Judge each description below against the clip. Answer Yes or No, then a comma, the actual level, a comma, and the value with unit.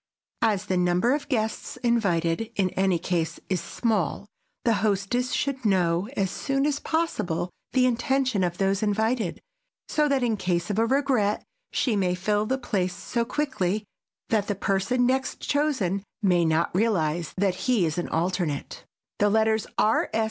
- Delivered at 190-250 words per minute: No, average, 160 wpm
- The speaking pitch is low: No, high, 205 Hz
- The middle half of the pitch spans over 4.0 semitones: Yes, average, 5.2 semitones